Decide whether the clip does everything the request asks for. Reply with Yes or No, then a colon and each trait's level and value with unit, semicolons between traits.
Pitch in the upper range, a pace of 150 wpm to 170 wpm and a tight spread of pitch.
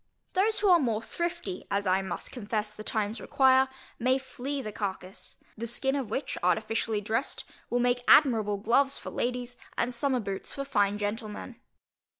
No: high, 235 Hz; average, 165 wpm; average, 4.2 semitones